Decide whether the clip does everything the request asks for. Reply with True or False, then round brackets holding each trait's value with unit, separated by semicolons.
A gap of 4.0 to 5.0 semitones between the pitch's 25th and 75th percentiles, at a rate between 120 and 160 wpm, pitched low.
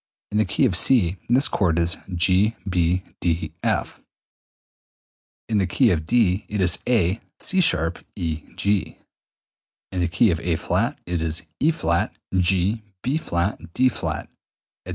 True (4.3 semitones; 140 wpm; 90 Hz)